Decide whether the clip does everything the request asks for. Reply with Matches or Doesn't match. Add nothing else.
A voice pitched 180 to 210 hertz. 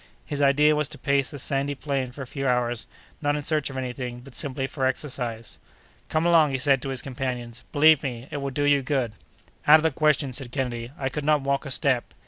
Doesn't match